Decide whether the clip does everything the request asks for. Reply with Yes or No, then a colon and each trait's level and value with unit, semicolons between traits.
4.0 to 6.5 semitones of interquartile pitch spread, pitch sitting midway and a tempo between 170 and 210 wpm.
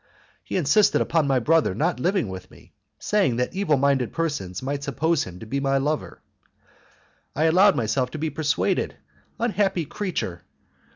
No: average, 5.0 semitones; medium, 145 Hz; average, 160 wpm